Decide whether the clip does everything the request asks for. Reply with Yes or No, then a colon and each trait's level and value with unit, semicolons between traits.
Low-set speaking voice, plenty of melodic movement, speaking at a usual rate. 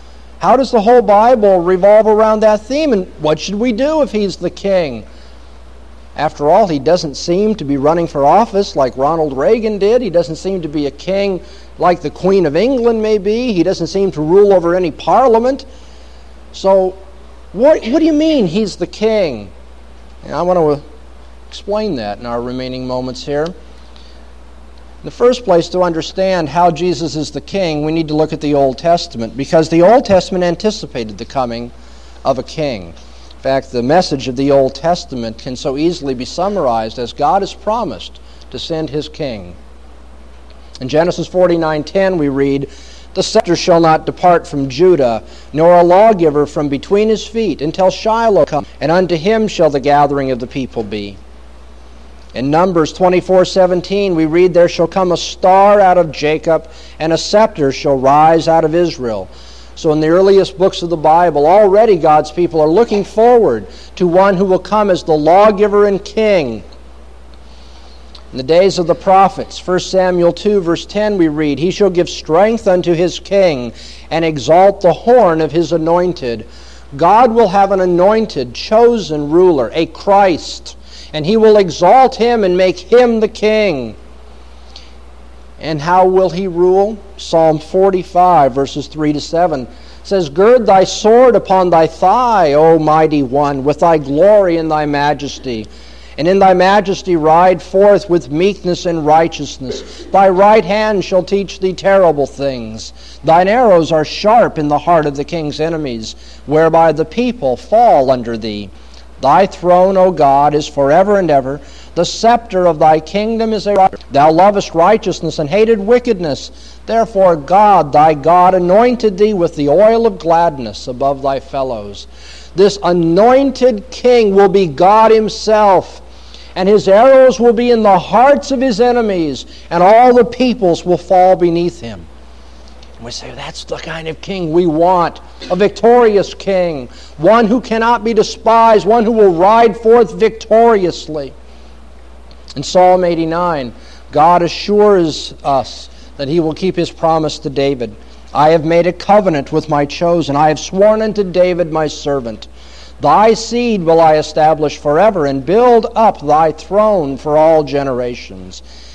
No: medium, 170 Hz; wide, 6.2 semitones; average, 165 wpm